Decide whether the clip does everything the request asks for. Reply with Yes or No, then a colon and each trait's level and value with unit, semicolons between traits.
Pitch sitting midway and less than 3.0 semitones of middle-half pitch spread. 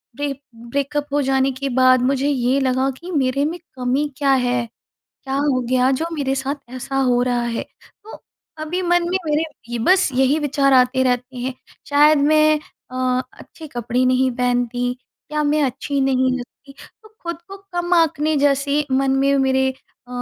No: very high, 270 Hz; narrow, 2.6 semitones